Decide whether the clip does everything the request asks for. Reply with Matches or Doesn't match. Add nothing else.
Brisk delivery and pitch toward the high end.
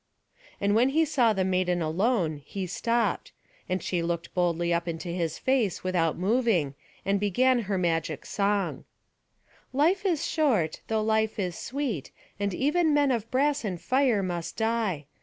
Doesn't match